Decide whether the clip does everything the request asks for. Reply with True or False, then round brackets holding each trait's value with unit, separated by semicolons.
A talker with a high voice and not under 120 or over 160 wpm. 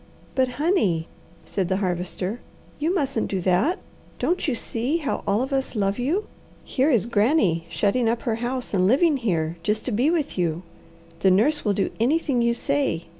False (235 Hz; 180 wpm)